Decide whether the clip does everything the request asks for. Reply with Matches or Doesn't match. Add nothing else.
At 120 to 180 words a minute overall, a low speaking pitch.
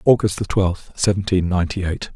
Matches